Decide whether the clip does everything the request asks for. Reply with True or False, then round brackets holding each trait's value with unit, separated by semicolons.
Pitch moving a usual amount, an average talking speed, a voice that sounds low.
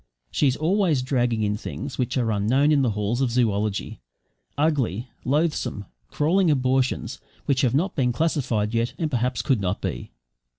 True (4.4 semitones; 165 wpm; 130 Hz)